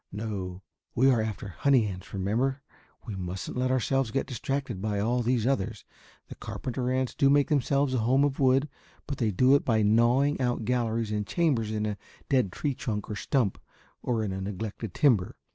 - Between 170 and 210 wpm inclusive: Yes, average, 190 wpm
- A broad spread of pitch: No, average, 4.2 semitones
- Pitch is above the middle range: No, low, 120 Hz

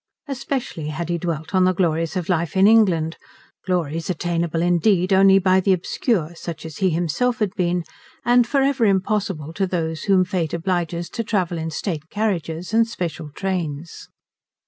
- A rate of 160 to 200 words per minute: Yes, average, 170 wpm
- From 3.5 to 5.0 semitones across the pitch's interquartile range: No, average, 3.0 semitones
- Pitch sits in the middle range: Yes, medium, 180 Hz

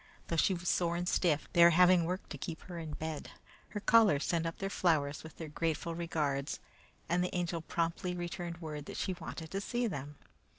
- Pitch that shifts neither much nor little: No, narrow, 2.0 semitones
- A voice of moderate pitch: Yes, medium, 170 Hz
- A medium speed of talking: No, fast, 210 wpm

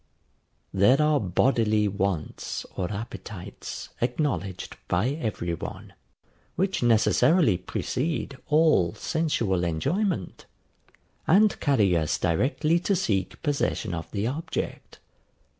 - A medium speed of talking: No, slow, 100 wpm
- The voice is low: Yes, low, 115 Hz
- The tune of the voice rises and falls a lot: Yes, wide, 8.3 semitones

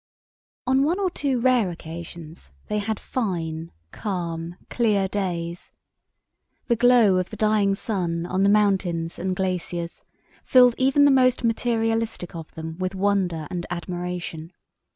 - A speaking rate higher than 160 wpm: No, slow, 135 wpm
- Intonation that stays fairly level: No, average, 4.8 semitones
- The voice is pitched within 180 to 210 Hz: Yes, high, 190 Hz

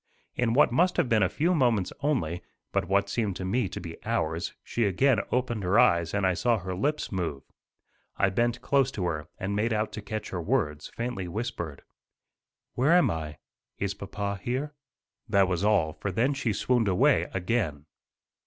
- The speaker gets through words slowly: No, average, 185 wpm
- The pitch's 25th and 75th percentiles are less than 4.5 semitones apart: No, average, 5.1 semitones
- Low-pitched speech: Yes, low, 100 Hz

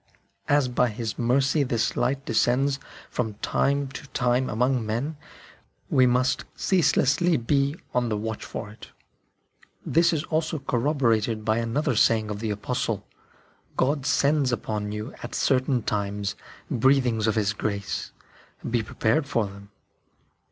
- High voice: No, low, 125 Hz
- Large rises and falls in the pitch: No, average, 4.0 semitones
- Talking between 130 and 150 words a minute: Yes, average, 140 wpm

